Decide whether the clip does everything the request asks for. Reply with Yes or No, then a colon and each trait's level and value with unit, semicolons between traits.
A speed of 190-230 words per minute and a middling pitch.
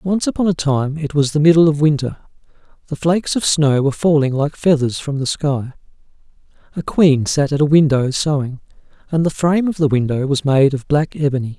Yes: average, 200 wpm; medium, 150 Hz